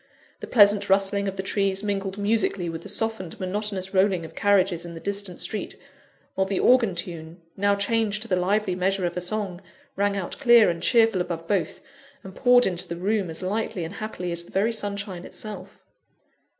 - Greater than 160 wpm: Yes, average, 190 wpm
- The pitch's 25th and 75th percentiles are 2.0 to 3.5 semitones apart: Yes, narrow, 2.5 semitones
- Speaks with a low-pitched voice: No, high, 195 Hz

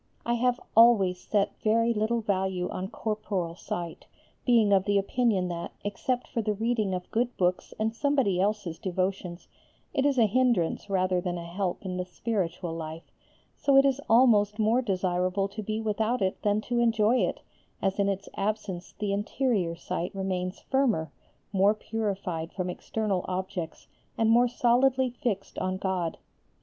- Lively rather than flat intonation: No, average, 3.9 semitones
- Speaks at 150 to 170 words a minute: Yes, average, 160 wpm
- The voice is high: Yes, high, 205 Hz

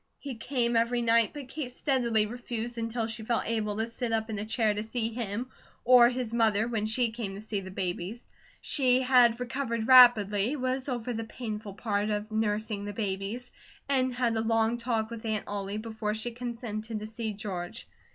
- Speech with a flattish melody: Yes, narrow, 2.2 semitones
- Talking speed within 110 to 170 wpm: No, average, 190 wpm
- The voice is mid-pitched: No, high, 225 Hz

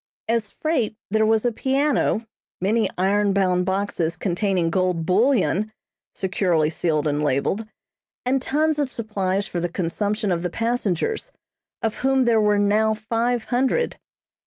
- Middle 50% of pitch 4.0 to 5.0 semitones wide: Yes, average, 4.3 semitones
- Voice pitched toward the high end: Yes, high, 210 Hz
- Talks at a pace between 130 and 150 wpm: Yes, average, 140 wpm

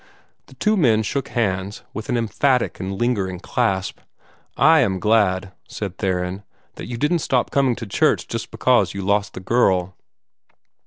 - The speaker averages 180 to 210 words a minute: No, average, 160 wpm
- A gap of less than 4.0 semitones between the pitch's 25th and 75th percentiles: No, average, 4.6 semitones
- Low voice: Yes, low, 105 Hz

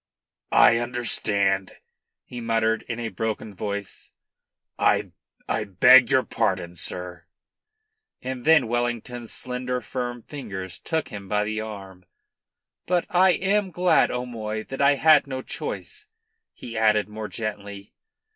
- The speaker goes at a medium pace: No, slow, 125 wpm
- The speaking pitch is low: Yes, low, 115 Hz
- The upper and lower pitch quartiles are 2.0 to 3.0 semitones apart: No, average, 3.6 semitones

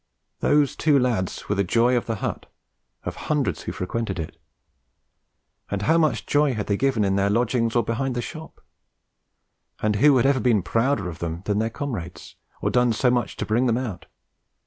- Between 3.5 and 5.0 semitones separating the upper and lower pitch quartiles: Yes, average, 4.3 semitones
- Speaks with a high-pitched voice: No, low, 115 Hz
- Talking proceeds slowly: No, average, 190 wpm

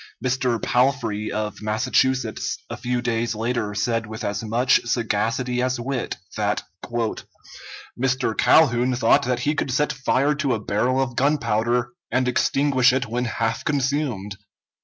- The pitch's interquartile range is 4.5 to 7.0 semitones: No, narrow, 2.5 semitones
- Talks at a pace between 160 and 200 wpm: No, average, 140 wpm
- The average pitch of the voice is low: Yes, low, 120 Hz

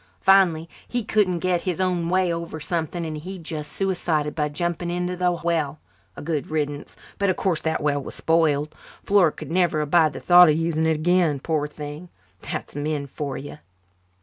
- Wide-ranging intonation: No, average, 2.8 semitones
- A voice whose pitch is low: No, medium, 165 Hz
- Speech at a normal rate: Yes, average, 185 wpm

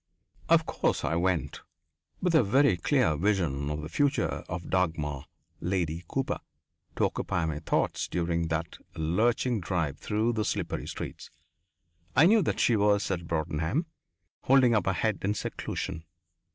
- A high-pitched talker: No, very low, 90 Hz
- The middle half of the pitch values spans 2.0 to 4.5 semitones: No, wide, 5.5 semitones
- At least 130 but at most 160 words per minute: Yes, average, 150 wpm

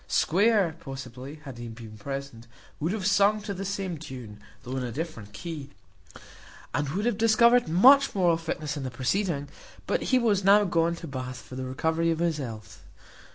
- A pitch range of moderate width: No, wide, 7.1 semitones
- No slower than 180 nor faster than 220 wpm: Yes, average, 185 wpm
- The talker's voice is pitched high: No, medium, 160 Hz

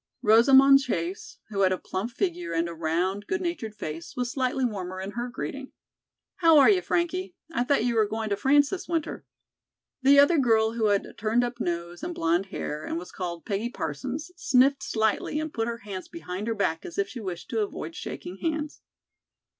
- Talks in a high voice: Yes, high, 225 Hz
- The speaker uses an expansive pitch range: Yes, wide, 6.6 semitones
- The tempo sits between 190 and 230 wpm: Yes, average, 200 wpm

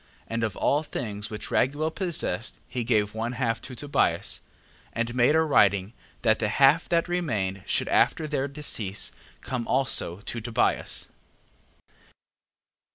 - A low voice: Yes, low, 120 Hz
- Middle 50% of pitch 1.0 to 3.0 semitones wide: No, average, 5.2 semitones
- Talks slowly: No, average, 145 wpm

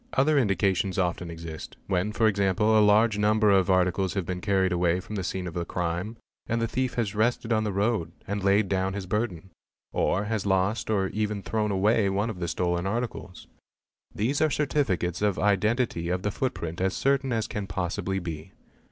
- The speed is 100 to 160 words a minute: No, average, 195 wpm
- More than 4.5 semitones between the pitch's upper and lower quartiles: No, average, 3.0 semitones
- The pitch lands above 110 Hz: No, low, 100 Hz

